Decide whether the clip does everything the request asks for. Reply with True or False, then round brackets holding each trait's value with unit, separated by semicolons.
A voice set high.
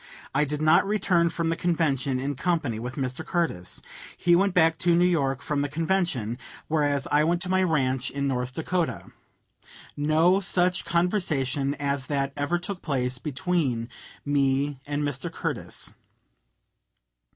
False (150 Hz)